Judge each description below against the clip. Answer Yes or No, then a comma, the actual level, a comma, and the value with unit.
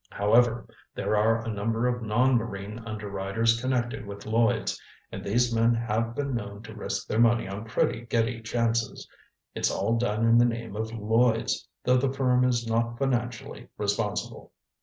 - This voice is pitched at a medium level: No, low, 115 Hz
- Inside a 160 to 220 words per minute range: Yes, average, 165 wpm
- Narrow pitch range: Yes, narrow, 1.8 semitones